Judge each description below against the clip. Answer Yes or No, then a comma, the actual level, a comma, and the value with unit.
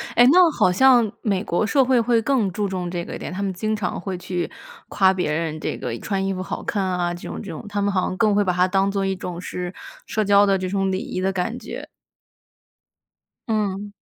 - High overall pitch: Yes, high, 195 Hz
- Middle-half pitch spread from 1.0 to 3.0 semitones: Yes, average, 2.7 semitones